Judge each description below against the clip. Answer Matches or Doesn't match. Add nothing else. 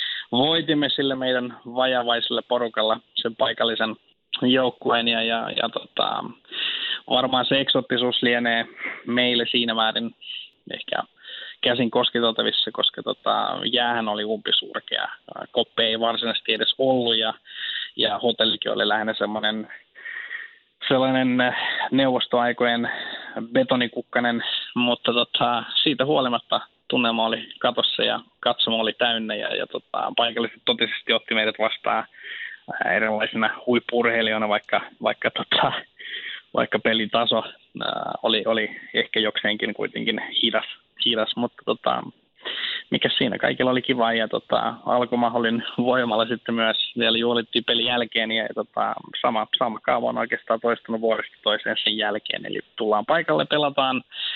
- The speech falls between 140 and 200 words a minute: Doesn't match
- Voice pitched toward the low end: Matches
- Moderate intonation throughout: Doesn't match